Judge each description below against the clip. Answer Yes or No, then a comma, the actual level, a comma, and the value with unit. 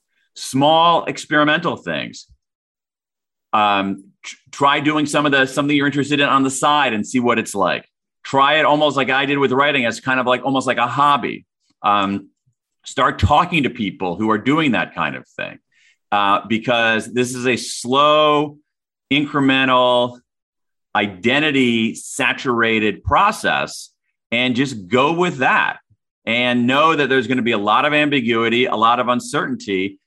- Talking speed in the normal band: Yes, average, 160 wpm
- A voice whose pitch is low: Yes, low, 130 Hz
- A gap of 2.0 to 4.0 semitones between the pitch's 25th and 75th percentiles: Yes, average, 3.7 semitones